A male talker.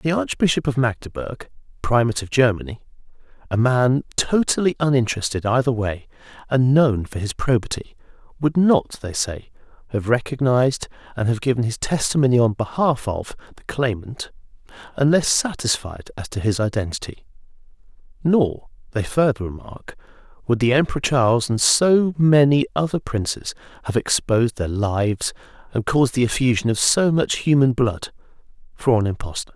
Yes: male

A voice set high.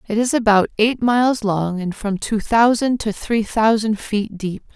Yes: high, 220 Hz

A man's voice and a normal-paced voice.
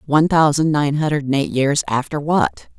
No: female; average, 170 wpm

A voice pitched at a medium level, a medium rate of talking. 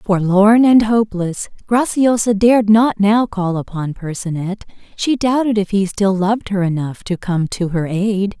No: high, 200 Hz; average, 165 wpm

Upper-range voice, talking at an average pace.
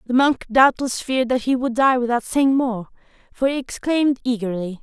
Yes: very high, 250 Hz; average, 185 wpm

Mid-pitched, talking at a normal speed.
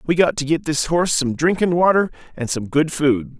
No: medium, 155 Hz; fast, 210 wpm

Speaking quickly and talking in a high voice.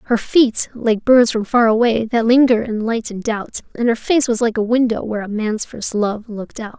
Yes: fast, 240 wpm; high, 225 Hz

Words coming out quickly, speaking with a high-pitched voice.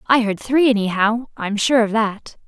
No: average, 195 wpm; high, 225 Hz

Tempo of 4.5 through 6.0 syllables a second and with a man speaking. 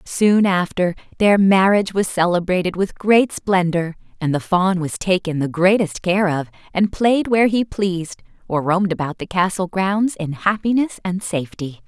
No: 4.8 syllables/s; female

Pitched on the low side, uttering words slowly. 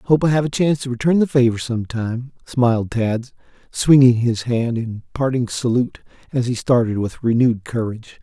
No: low, 125 Hz; average, 180 wpm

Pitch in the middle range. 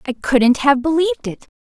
No: very high, 285 Hz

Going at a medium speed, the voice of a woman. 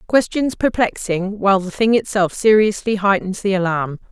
Yes: average, 145 wpm; female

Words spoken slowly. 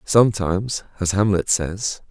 Yes: slow, 115 wpm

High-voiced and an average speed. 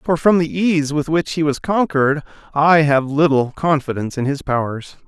No: medium, 150 Hz; average, 190 wpm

